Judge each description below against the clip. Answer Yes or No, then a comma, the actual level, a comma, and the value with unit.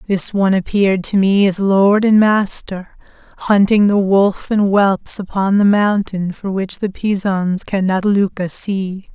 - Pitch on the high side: Yes, high, 195 Hz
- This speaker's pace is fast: No, average, 160 wpm